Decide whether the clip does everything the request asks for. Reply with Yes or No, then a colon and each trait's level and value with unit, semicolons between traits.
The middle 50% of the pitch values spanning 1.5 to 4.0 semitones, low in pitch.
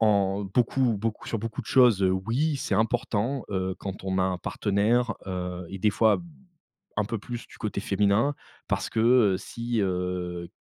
Yes: average, 3.7 semitones; low, 105 Hz